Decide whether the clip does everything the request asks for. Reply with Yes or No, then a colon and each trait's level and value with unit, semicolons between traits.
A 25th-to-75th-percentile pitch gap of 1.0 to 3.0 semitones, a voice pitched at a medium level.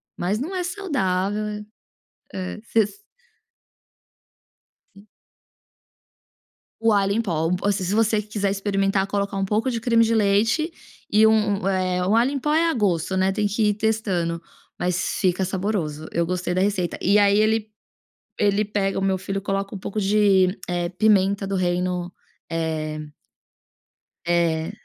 No: average, 2.7 semitones; high, 200 Hz